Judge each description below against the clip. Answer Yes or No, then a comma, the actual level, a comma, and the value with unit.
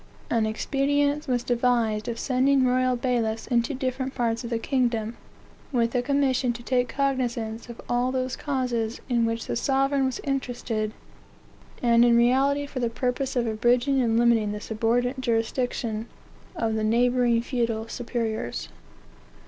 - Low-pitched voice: No, high, 245 Hz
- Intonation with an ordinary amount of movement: No, narrow, 2.2 semitones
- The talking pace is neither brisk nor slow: Yes, average, 150 wpm